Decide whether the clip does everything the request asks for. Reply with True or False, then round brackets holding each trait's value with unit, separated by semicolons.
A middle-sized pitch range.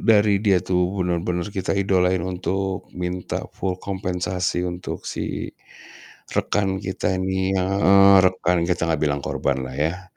False (1.4 semitones)